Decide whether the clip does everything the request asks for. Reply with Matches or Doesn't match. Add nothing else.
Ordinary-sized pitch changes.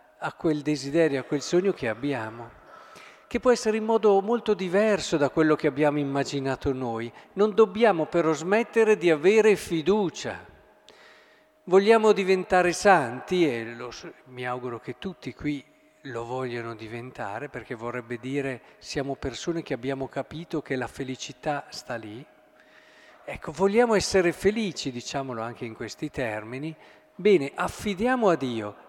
Doesn't match